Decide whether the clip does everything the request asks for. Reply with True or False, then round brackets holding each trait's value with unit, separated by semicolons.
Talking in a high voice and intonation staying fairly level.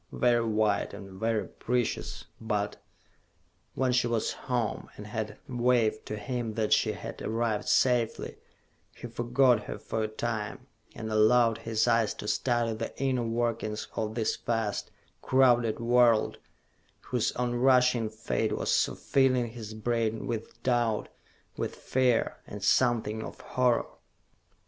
False (115 Hz; 2.0 semitones)